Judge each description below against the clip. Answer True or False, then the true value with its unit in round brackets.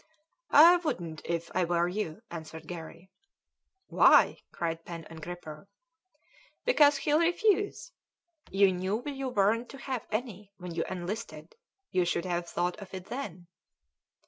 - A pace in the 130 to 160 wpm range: True (140 wpm)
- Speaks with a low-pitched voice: False (185 Hz)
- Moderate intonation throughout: False (6.4 semitones)